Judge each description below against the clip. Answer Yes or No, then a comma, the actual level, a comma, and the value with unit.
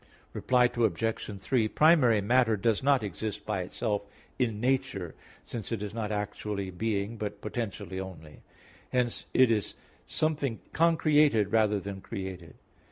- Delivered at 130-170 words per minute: Yes, slow, 135 wpm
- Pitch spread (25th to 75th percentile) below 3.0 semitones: No, average, 3.6 semitones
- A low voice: Yes, low, 110 Hz